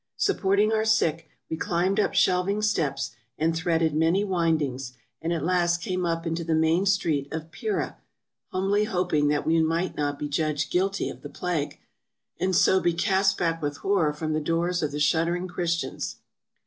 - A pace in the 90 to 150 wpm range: No, average, 175 wpm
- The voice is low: No, medium, 170 Hz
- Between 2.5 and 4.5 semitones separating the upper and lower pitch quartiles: Yes, average, 2.8 semitones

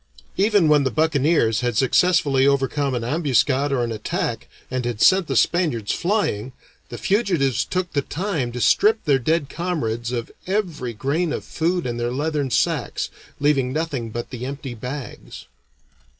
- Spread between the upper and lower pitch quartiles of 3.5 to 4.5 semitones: No, average, 5.2 semitones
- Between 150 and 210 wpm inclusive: Yes, average, 160 wpm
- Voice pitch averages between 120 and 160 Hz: Yes, medium, 140 Hz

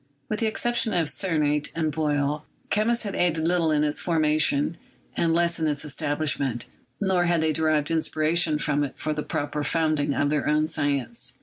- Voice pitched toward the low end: No, medium, 155 Hz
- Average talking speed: Yes, average, 185 wpm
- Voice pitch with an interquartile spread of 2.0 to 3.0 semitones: Yes, narrow, 2.5 semitones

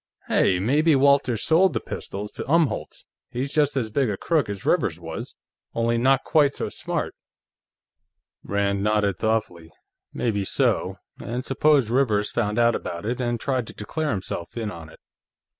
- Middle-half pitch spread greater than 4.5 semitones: Yes, average, 5.0 semitones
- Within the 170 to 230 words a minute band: No, average, 160 wpm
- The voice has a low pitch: Yes, low, 115 Hz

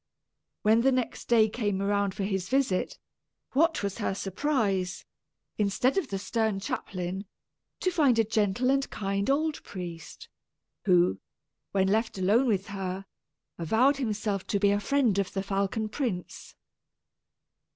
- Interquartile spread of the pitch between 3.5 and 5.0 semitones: Yes, average, 4.2 semitones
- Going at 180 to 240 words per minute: No, average, 140 wpm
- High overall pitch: Yes, high, 205 Hz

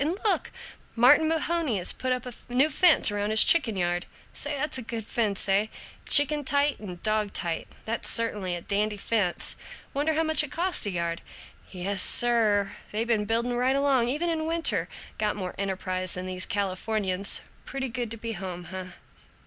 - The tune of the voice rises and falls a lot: Yes, wide, 6.0 semitones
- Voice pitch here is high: Yes, high, 225 Hz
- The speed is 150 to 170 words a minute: No, average, 180 wpm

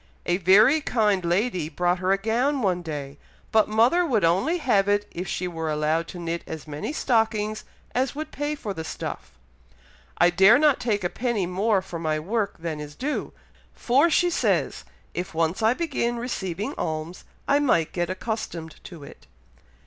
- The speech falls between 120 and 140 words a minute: No, average, 180 wpm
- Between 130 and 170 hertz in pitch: No, high, 195 Hz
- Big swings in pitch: Yes, wide, 6.1 semitones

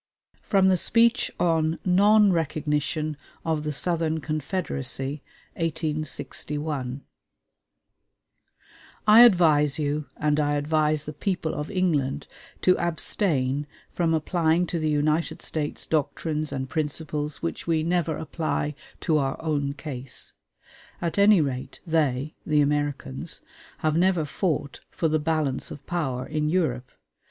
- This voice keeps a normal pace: No, slow, 125 wpm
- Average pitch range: No, narrow, 2.3 semitones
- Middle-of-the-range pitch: Yes, medium, 155 Hz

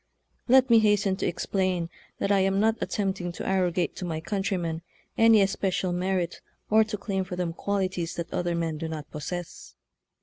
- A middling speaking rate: Yes, average, 170 wpm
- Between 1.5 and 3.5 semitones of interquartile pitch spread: Yes, narrow, 2.6 semitones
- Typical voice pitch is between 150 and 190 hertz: Yes, medium, 185 Hz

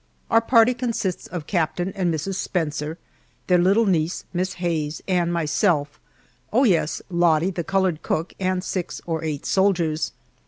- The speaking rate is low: No, average, 150 wpm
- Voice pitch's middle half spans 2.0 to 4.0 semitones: Yes, average, 3.2 semitones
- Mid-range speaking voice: Yes, medium, 175 Hz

